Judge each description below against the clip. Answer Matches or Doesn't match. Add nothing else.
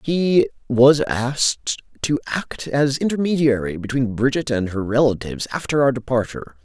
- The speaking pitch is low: Matches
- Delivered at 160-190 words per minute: Doesn't match